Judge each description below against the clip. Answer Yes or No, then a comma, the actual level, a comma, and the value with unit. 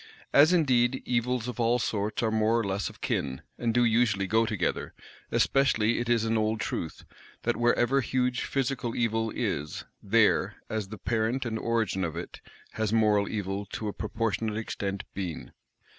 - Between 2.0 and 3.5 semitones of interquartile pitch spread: Yes, narrow, 2.5 semitones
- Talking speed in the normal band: Yes, average, 170 wpm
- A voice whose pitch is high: No, low, 110 Hz